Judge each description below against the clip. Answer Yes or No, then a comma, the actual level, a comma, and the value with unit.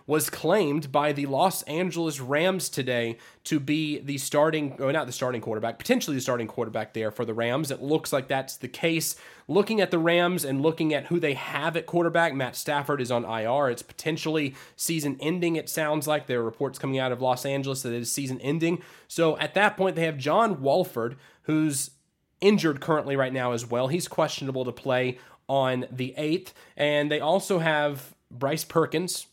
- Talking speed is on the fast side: No, average, 195 wpm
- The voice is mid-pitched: Yes, medium, 145 Hz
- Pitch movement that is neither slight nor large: Yes, average, 3.7 semitones